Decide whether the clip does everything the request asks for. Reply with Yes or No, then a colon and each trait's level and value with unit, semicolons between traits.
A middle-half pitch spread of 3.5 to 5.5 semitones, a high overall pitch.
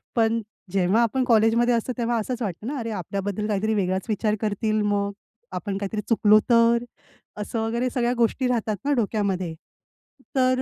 No: average, 2.7 semitones; high, 220 Hz